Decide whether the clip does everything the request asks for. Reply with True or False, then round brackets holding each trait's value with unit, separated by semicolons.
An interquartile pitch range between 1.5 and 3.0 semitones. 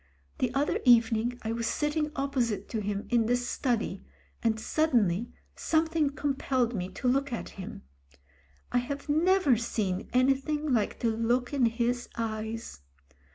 False (3.7 semitones)